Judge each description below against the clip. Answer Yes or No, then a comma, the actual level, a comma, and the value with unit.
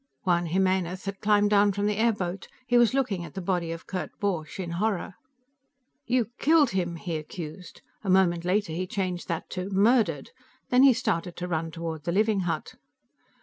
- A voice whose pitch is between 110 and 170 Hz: No, medium, 185 Hz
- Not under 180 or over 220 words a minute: Yes, average, 185 wpm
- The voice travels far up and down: No, average, 3.3 semitones